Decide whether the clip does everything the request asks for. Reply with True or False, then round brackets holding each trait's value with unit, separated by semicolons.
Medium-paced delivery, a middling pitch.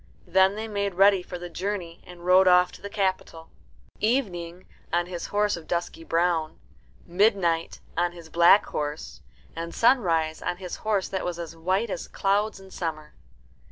True (165 wpm; 180 Hz)